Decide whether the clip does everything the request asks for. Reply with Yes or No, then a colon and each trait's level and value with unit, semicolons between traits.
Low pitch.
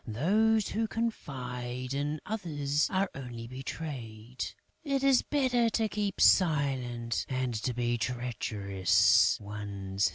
Yes: low, 130 Hz